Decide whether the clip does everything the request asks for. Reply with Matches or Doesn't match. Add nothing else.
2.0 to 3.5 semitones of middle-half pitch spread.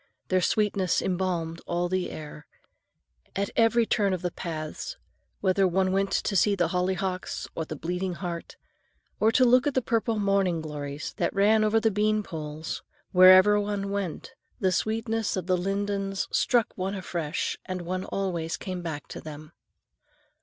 Matches